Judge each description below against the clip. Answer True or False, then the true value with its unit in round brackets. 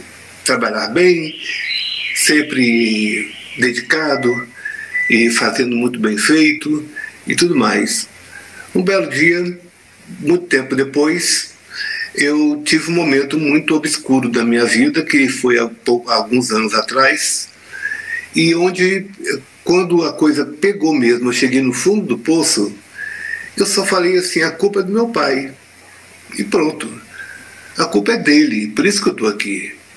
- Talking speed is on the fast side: False (135 wpm)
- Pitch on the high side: False (155 Hz)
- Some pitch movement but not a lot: False (7.9 semitones)